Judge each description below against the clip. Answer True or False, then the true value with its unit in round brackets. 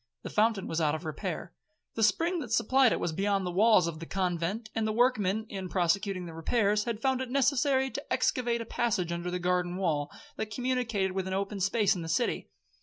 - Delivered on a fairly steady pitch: False (4.6 semitones)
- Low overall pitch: False (200 Hz)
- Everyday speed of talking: False (215 wpm)